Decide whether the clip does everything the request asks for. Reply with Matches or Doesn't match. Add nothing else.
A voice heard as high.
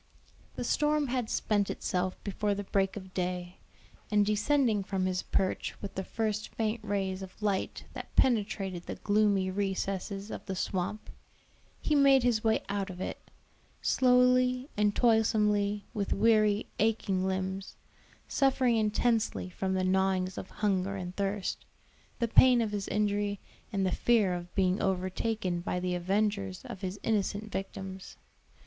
Matches